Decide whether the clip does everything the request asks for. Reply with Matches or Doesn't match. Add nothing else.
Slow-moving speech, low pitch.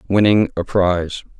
Matches